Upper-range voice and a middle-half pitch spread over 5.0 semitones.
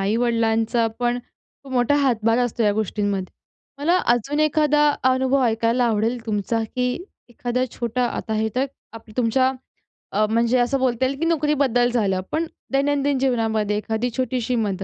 No: high, 240 Hz; average, 2.9 semitones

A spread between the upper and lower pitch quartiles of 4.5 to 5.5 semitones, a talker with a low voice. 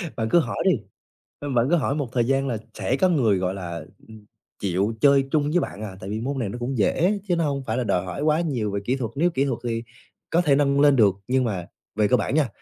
Yes: average, 5.2 semitones; low, 130 Hz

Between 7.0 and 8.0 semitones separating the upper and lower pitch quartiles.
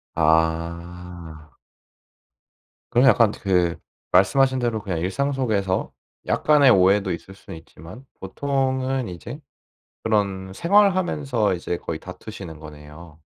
Yes: wide, 7.3 semitones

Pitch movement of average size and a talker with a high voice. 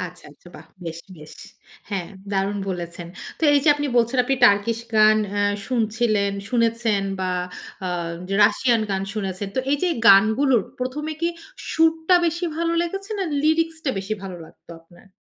No: wide, 6.8 semitones; high, 230 Hz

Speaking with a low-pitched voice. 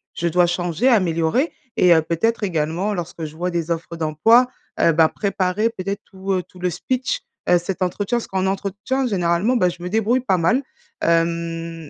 No: medium, 180 Hz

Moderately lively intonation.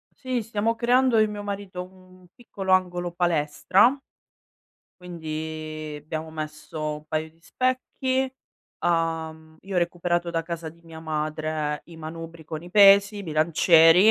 Yes: average, 3.8 semitones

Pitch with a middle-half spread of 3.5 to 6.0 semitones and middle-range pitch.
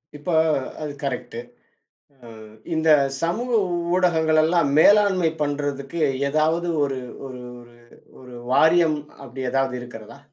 Yes: average, 3.8 semitones; medium, 150 Hz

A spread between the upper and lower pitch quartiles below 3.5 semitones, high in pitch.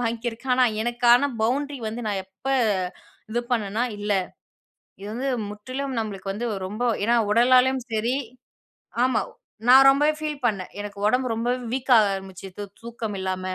No: average, 3.8 semitones; high, 235 Hz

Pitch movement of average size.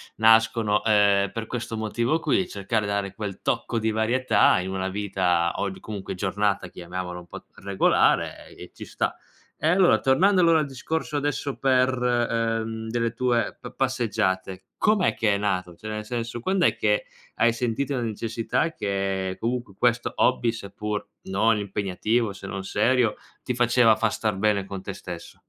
Yes: average, 3.6 semitones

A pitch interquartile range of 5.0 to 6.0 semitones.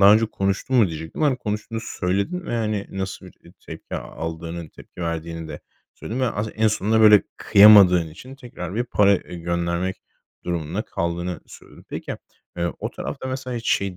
No: average, 4.4 semitones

